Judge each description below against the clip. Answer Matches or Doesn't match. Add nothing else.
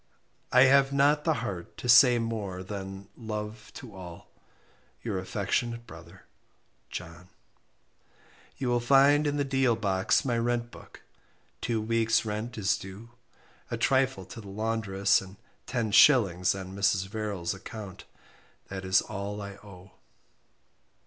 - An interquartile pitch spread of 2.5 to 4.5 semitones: Matches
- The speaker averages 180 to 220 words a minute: Doesn't match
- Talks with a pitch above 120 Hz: Doesn't match